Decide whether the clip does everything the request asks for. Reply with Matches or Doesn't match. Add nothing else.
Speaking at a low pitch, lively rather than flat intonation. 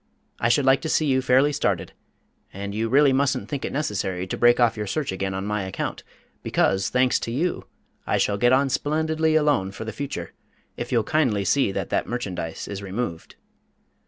Matches